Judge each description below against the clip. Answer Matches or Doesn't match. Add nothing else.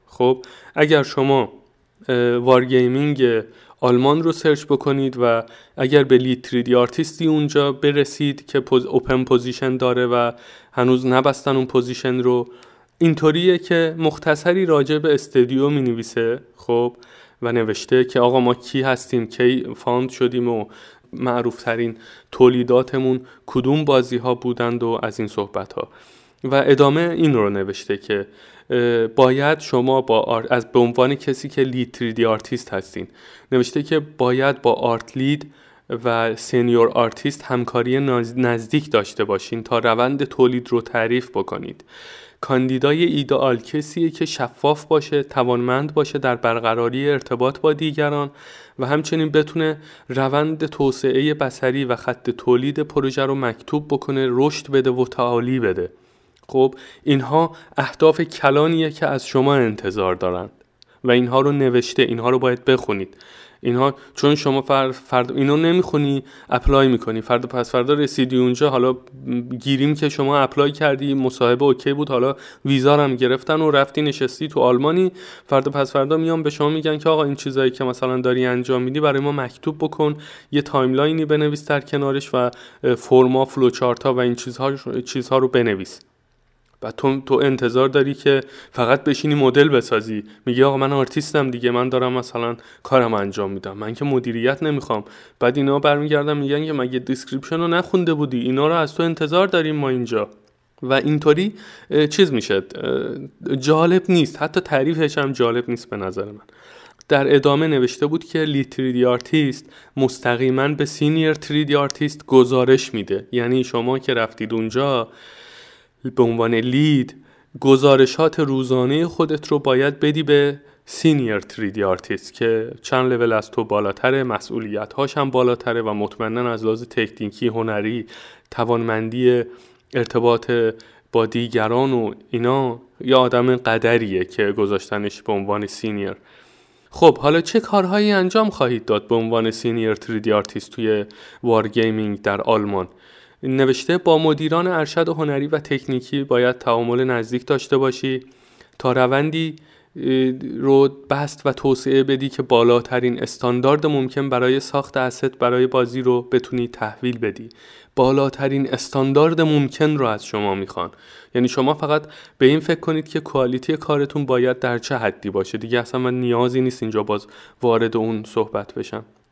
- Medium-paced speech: Matches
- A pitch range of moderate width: Matches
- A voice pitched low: Matches